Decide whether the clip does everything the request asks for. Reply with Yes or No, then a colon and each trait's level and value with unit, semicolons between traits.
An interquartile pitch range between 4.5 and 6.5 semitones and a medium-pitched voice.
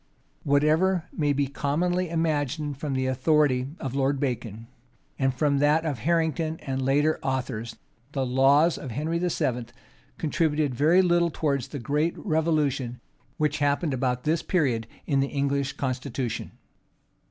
No: average, 3.2 semitones; medium, 145 Hz